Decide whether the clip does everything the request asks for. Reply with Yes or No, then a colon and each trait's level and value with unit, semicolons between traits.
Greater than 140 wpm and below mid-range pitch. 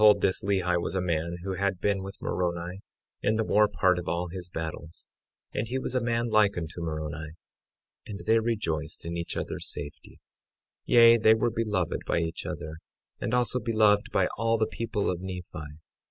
Yes: average, 190 wpm; very low, 95 Hz